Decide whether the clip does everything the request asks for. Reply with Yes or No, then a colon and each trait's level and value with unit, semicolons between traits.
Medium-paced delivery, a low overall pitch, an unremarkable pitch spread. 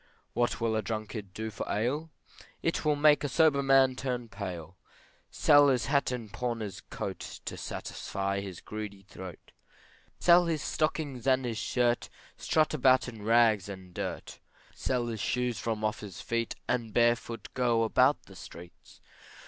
Yes: average, 160 wpm; low, 120 Hz; average, 3.8 semitones